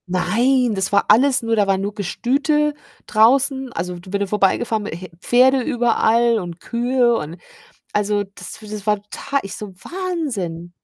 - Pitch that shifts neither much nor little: Yes, average, 4.8 semitones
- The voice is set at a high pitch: Yes, high, 220 Hz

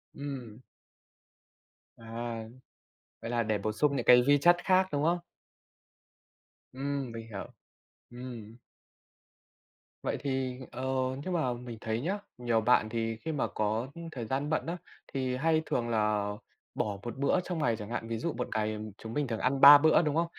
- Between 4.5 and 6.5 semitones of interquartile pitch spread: No, average, 4.1 semitones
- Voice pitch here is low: Yes, low, 125 Hz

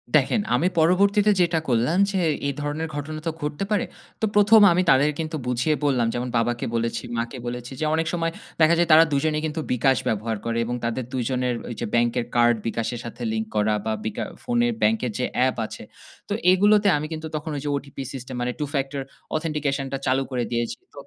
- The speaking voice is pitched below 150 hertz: Yes, medium, 140 Hz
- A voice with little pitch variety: No, average, 5.0 semitones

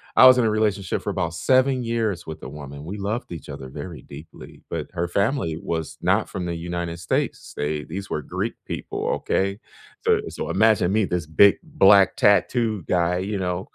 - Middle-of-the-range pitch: No, very low, 90 Hz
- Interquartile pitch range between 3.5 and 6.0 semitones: Yes, average, 4.0 semitones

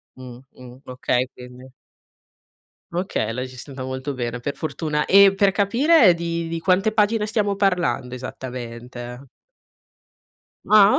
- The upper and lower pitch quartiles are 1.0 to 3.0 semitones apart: No, wide, 7.7 semitones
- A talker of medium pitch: Yes, medium, 145 Hz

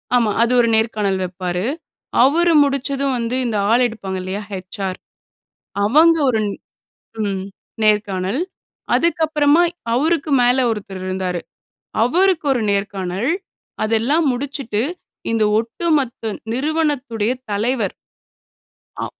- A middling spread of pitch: No, wide, 5.9 semitones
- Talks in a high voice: Yes, high, 230 Hz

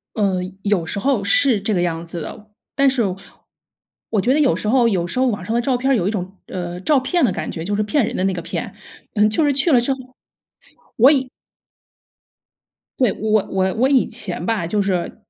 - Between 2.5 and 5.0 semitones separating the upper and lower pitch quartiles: No, wide, 5.5 semitones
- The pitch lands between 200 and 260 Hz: Yes, high, 215 Hz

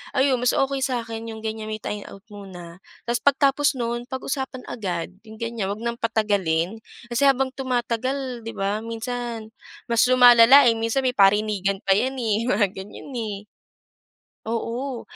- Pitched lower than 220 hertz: No, high, 230 Hz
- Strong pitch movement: No, average, 3.3 semitones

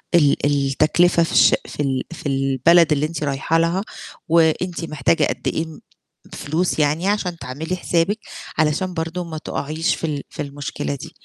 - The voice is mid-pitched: Yes, medium, 160 Hz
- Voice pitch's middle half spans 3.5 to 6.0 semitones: No, average, 2.8 semitones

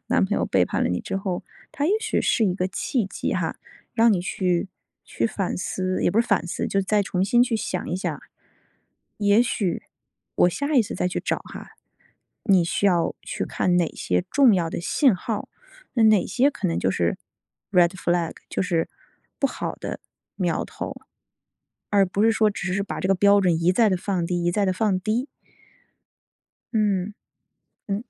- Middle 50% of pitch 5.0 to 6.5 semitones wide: No, average, 3.3 semitones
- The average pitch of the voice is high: Yes, high, 195 Hz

